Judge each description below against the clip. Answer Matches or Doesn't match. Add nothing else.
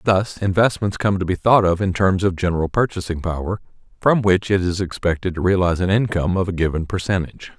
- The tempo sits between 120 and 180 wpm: Doesn't match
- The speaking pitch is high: Doesn't match